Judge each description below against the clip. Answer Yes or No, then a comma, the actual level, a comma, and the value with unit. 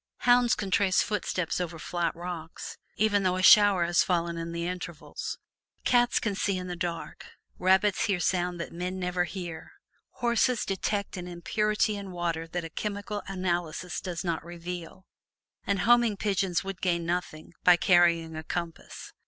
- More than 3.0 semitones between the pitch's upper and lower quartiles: No, narrow, 2.6 semitones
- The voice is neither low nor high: Yes, medium, 180 Hz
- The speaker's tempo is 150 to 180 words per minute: Yes, average, 160 wpm